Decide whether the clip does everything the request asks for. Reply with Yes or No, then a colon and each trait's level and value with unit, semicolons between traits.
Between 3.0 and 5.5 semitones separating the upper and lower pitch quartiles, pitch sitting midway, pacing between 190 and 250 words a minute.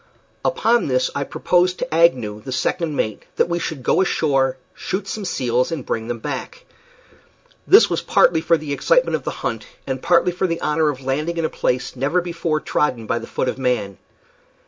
Yes: average, 5.2 semitones; medium, 150 Hz; average, 195 wpm